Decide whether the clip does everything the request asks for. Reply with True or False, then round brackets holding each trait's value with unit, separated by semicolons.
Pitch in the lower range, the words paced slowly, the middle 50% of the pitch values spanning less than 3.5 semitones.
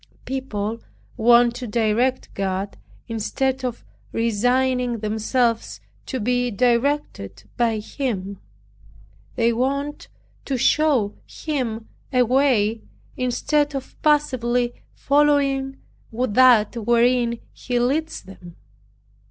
False (245 Hz; 95 wpm; 3.0 semitones)